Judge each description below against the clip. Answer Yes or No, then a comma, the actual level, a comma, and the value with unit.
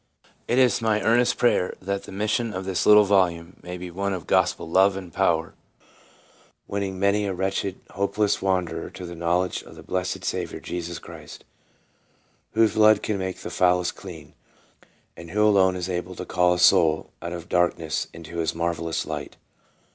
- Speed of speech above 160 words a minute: Yes, average, 175 wpm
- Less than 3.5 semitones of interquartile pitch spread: Yes, narrow, 2.4 semitones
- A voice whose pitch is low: Yes, very low, 95 Hz